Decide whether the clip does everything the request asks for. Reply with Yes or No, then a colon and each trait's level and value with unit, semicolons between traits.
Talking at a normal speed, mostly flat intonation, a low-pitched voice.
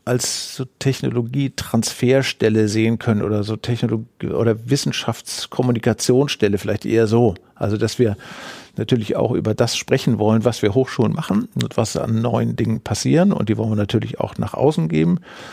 Yes: average, 160 wpm; narrow, 2.3 semitones; low, 115 Hz